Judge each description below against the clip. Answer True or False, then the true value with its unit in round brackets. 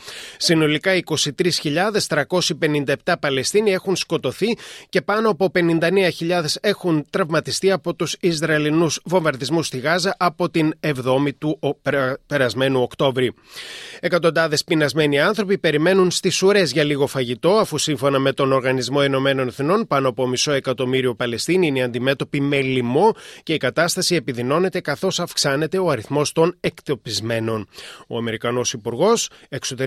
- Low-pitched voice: False (155 Hz)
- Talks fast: False (125 wpm)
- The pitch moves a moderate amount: True (4.8 semitones)